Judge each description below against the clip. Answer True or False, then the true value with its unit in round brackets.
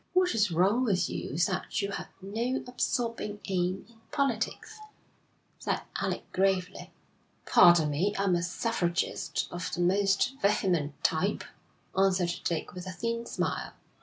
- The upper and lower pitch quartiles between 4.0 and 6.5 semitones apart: True (4.3 semitones)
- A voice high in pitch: True (195 Hz)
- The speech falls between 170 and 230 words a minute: False (145 wpm)